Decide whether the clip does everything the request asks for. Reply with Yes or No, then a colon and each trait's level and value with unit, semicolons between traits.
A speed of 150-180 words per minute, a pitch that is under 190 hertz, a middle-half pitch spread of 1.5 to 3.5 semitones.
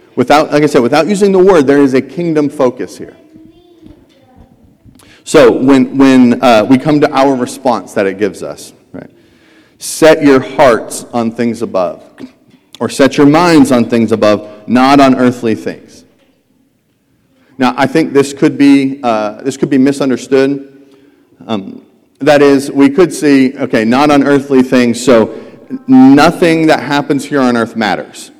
Yes: average, 160 wpm; medium, 140 Hz; average, 2.9 semitones